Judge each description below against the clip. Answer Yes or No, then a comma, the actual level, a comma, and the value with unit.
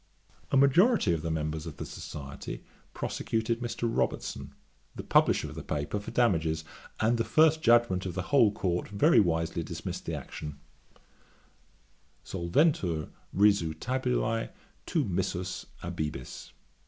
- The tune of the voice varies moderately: No, wide, 6.8 semitones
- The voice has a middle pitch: No, very low, 95 Hz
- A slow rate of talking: Yes, slow, 130 wpm